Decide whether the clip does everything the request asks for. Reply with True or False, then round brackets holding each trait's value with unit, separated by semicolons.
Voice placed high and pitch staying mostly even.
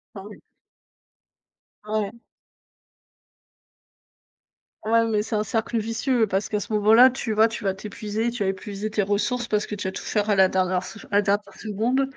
True (210 Hz; 1.9 semitones)